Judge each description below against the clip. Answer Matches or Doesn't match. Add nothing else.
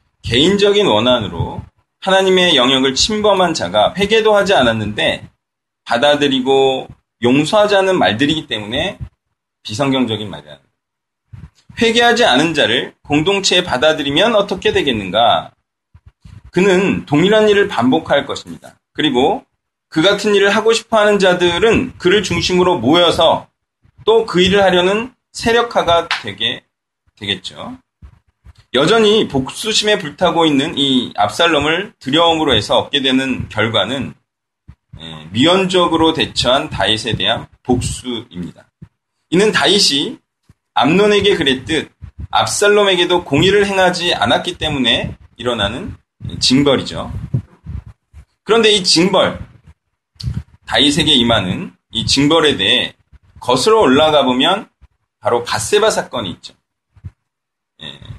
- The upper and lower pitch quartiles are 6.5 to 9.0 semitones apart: Matches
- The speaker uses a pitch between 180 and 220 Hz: Doesn't match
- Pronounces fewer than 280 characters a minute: Matches